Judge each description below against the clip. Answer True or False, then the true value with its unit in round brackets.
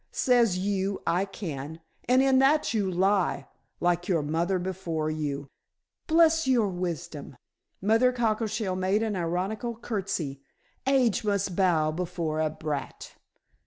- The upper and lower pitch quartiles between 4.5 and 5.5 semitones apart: True (5.1 semitones)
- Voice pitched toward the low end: False (190 Hz)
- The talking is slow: True (125 wpm)